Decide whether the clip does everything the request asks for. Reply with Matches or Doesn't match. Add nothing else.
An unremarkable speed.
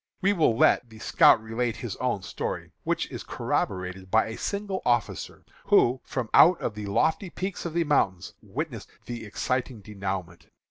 Matches